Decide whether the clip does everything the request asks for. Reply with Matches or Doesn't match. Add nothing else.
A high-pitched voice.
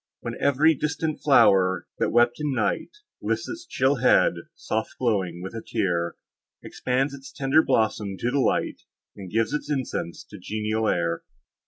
Doesn't match